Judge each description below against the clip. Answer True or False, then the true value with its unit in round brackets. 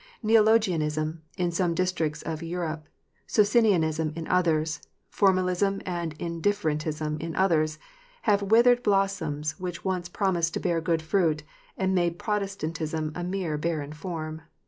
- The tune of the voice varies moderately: True (3.6 semitones)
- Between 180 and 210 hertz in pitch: False (170 Hz)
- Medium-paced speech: False (125 wpm)